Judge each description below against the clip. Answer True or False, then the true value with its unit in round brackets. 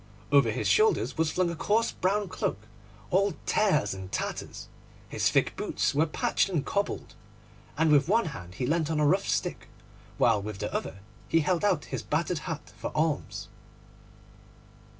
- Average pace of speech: True (170 wpm)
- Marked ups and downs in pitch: False (5.0 semitones)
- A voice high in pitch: False (160 Hz)